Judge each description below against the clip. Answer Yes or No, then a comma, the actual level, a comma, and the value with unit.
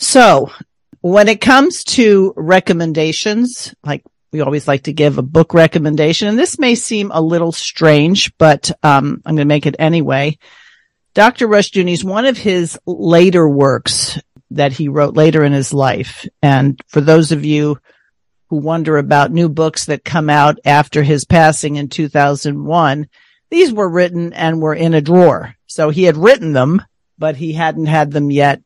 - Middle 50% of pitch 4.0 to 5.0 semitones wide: No, average, 3.3 semitones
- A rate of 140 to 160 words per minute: No, average, 170 wpm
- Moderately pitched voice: Yes, medium, 160 Hz